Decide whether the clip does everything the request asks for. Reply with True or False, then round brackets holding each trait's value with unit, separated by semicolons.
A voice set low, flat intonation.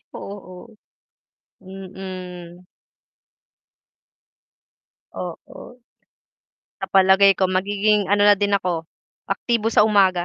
False (195 Hz; 1.9 semitones)